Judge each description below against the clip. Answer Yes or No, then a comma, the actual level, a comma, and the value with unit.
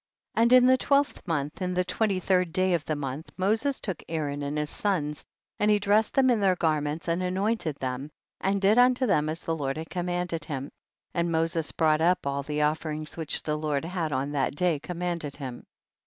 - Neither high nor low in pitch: Yes, medium, 165 Hz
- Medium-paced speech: No, fast, 210 wpm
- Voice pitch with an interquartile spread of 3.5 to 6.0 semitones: Yes, average, 4.2 semitones